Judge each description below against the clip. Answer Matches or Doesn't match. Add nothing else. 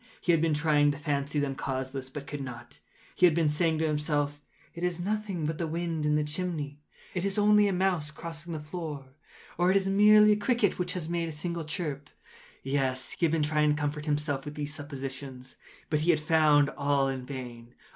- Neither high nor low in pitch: Matches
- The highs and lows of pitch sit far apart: Doesn't match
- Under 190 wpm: Doesn't match